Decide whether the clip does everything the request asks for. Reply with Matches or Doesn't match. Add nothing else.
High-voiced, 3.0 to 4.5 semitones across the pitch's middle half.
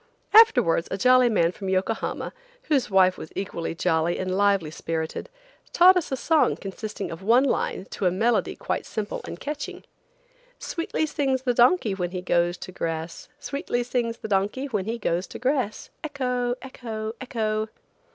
Doesn't match